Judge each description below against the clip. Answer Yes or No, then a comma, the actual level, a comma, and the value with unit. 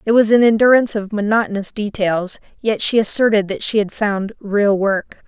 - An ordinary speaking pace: Yes, average, 180 wpm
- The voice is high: Yes, high, 210 Hz